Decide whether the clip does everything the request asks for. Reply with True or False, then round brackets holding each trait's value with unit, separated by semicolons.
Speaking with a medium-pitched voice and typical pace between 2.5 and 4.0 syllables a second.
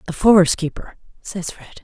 False (175 Hz; 5.3 syllables/s)